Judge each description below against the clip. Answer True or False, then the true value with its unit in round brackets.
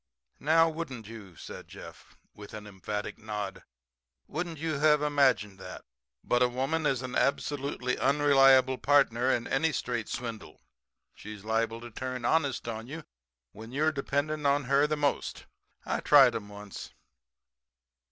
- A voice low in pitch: True (130 Hz)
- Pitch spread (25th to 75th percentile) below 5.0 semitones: True (4.5 semitones)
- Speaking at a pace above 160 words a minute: False (150 wpm)